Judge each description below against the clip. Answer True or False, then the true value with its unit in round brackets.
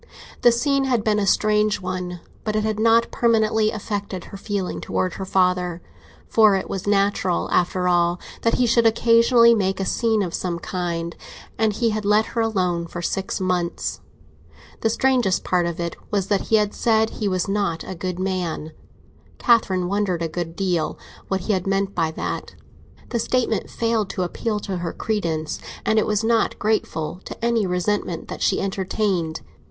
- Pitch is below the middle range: False (195 Hz)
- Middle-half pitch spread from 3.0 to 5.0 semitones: True (3.4 semitones)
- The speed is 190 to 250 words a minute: False (180 wpm)